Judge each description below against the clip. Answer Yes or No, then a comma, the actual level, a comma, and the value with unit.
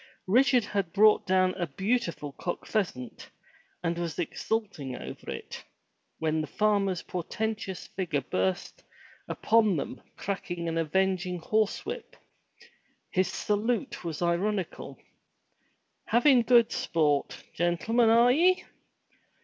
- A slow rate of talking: Yes, slow, 110 wpm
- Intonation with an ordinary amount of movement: Yes, average, 4.6 semitones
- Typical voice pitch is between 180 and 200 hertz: Yes, high, 190 Hz